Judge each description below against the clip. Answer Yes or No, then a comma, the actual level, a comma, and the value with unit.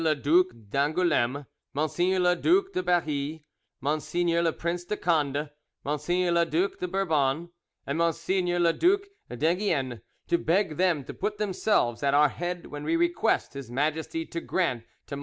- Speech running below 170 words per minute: Yes, average, 160 wpm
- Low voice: No, medium, 165 Hz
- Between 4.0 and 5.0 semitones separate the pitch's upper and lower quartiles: No, average, 3.4 semitones